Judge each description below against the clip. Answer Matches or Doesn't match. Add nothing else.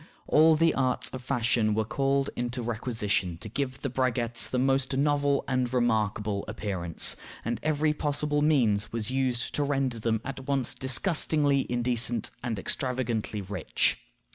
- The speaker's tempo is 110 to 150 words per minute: Matches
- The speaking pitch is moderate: Doesn't match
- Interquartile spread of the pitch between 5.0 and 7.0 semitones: Doesn't match